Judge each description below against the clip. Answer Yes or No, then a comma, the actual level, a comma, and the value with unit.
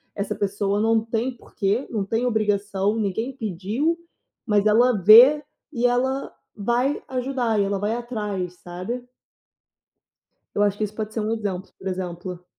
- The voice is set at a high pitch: Yes, high, 215 Hz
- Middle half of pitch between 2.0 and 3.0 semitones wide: No, average, 3.4 semitones